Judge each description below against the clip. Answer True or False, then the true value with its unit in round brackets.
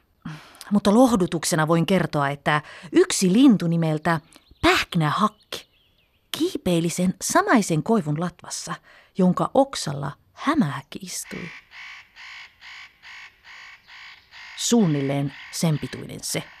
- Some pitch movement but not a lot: False (6.6 semitones)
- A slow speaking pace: True (80 wpm)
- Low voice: False (180 Hz)